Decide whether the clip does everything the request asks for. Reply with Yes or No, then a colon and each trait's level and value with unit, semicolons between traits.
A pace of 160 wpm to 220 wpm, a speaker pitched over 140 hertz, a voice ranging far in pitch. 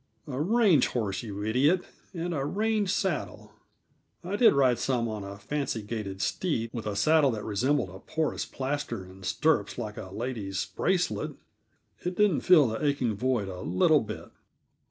No: average, 165 wpm; low, 125 Hz; wide, 7.0 semitones